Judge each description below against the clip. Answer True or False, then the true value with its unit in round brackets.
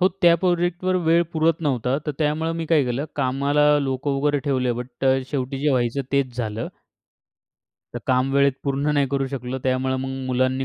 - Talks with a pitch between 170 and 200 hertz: False (140 Hz)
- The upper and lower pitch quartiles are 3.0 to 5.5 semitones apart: False (2.6 semitones)